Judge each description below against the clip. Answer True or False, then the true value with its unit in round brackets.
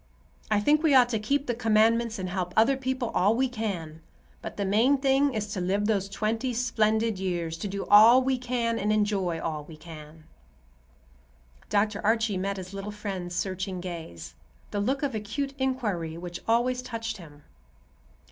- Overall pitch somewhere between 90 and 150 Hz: False (210 Hz)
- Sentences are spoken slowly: False (175 wpm)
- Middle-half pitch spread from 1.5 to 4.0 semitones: False (4.4 semitones)